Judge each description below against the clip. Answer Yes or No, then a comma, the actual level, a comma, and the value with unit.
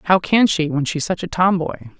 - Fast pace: Yes, fast, 240 wpm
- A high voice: No, medium, 170 Hz